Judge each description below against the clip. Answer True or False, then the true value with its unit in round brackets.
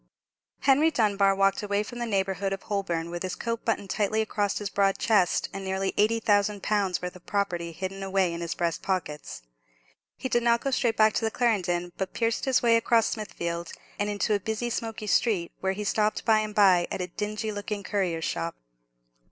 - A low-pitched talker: False (200 Hz)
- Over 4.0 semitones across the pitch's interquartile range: False (2.8 semitones)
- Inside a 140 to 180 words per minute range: False (200 wpm)